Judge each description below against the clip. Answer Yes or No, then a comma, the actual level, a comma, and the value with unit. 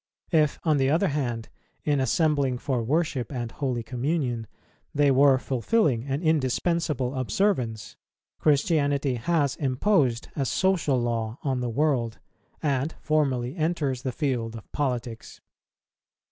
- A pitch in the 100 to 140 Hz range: Yes, low, 135 Hz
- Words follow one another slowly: Yes, slow, 125 wpm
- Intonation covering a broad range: No, average, 3.8 semitones